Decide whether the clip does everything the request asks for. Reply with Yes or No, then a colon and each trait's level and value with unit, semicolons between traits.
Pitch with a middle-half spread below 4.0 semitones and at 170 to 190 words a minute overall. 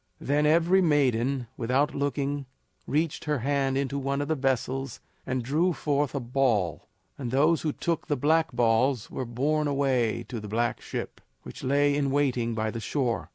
Yes: average, 3.0 semitones; average, 175 wpm